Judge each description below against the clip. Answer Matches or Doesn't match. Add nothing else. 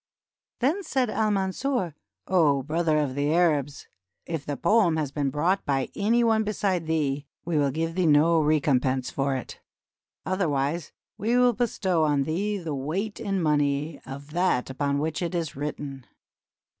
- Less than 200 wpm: Matches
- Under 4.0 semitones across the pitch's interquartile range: Doesn't match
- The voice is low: Doesn't match